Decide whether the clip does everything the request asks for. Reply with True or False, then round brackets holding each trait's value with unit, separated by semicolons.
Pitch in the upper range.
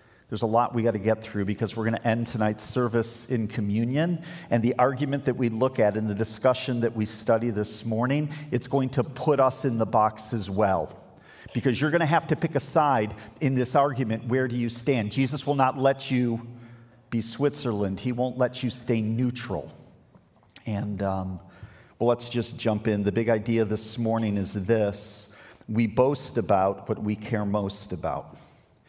False (115 Hz)